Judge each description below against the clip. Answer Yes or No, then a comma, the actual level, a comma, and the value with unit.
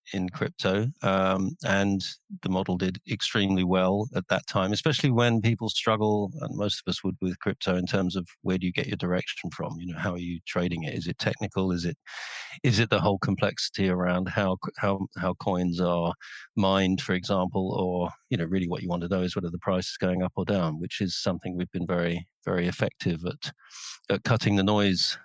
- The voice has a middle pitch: No, very low, 95 Hz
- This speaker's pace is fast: Yes, fast, 215 wpm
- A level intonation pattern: Yes, narrow, 1.8 semitones